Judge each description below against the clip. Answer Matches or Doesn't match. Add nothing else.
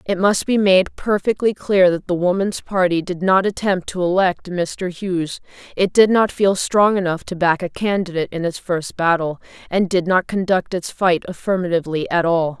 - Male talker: Doesn't match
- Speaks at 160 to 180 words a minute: Doesn't match